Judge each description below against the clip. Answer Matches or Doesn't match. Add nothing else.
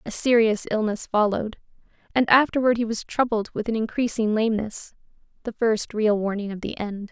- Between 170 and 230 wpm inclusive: Doesn't match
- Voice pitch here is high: Matches